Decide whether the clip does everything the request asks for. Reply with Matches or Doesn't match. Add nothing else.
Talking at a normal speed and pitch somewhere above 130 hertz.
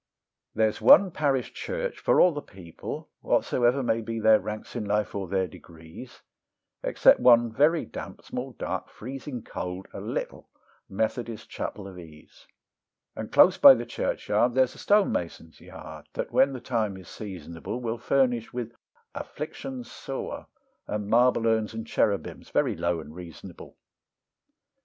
Doesn't match